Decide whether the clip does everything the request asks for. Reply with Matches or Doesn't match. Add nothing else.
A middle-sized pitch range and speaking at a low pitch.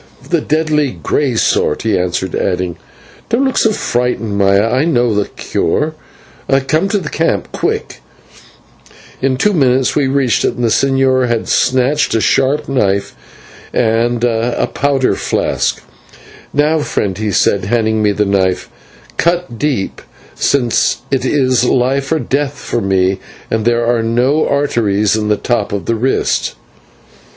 Matches